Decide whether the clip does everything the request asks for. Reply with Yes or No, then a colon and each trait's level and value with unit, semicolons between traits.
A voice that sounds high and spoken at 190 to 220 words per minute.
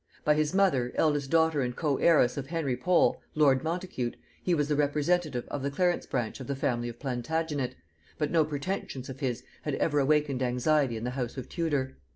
No: medium, 145 Hz; average, 195 wpm